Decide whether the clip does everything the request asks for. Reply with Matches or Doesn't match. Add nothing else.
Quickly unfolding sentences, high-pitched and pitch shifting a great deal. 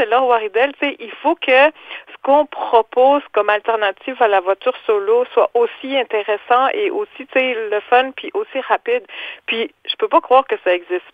Doesn't match